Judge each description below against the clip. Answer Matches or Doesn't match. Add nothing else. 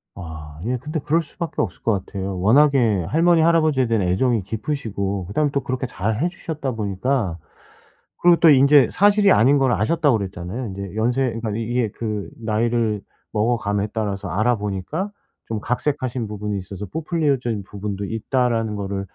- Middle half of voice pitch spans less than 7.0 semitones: Matches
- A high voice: Doesn't match